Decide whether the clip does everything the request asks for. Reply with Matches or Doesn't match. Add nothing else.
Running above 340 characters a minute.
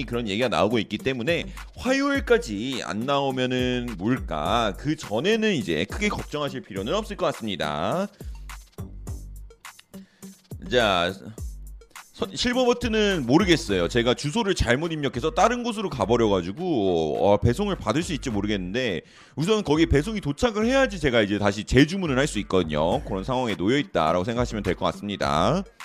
Doesn't match